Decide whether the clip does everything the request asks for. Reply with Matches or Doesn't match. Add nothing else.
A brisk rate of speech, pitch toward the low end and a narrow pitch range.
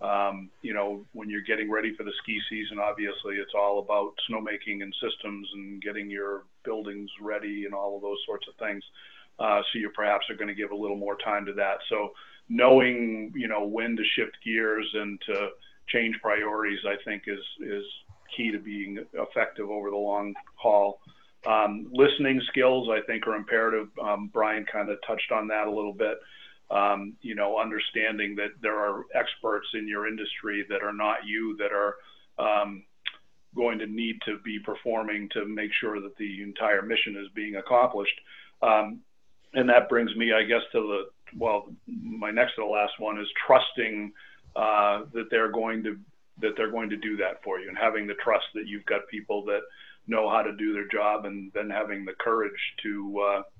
Doesn't match